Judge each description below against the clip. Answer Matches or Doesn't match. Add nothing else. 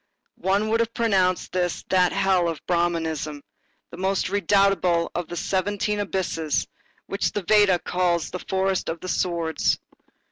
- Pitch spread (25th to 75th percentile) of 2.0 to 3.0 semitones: Matches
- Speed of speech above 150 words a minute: Doesn't match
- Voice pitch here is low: Doesn't match